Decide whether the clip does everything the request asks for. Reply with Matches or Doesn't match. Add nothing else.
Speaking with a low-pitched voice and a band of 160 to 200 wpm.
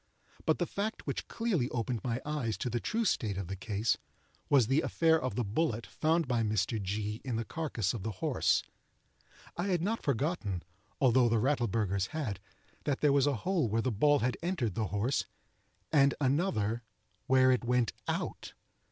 Matches